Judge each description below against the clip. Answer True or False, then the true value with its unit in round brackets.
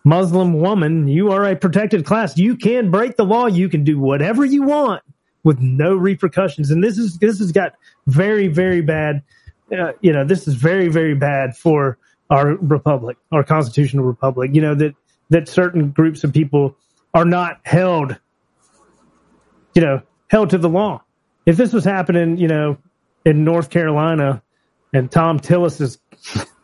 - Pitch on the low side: False (165 Hz)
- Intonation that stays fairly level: False (4.4 semitones)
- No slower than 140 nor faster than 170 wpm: True (165 wpm)